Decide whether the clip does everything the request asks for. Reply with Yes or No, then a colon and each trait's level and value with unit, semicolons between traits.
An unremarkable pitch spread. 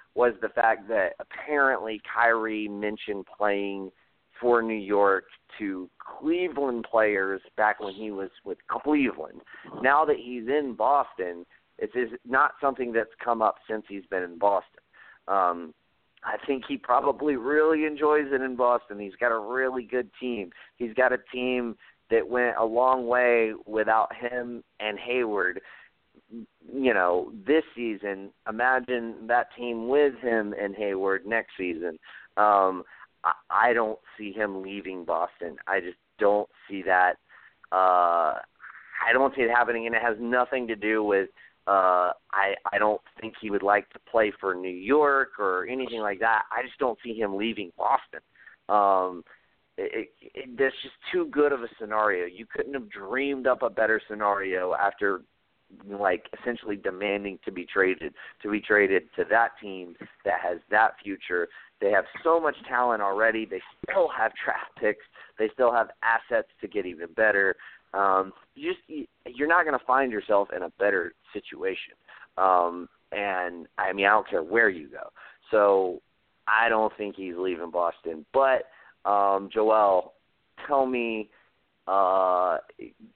Yes: average, 4.2 semitones